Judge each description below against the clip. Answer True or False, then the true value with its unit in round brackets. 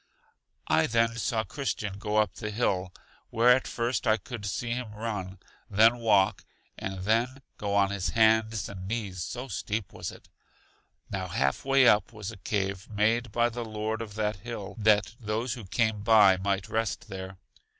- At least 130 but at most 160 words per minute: False (175 wpm)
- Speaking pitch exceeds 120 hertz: False (110 Hz)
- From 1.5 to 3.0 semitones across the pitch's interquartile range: True (2.6 semitones)